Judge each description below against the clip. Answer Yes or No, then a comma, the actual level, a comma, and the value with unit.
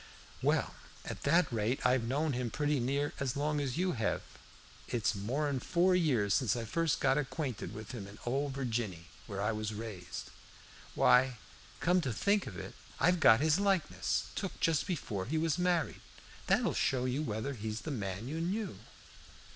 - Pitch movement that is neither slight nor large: No, wide, 6.1 semitones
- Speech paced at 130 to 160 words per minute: No, average, 180 wpm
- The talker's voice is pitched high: No, low, 130 Hz